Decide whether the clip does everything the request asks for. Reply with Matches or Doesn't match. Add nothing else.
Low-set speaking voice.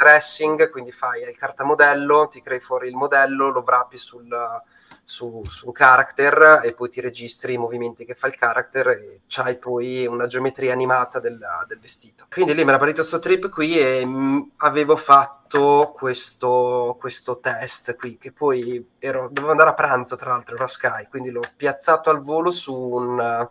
Matches